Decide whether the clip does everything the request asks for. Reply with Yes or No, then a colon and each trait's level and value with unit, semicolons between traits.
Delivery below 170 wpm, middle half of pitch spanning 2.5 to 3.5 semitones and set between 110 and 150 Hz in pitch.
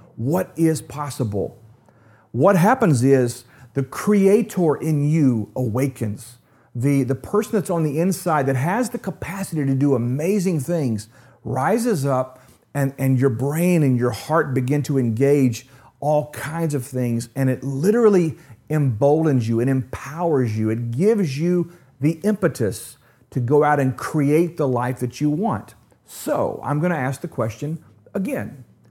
No: average, 150 wpm; average, 4.6 semitones; medium, 140 Hz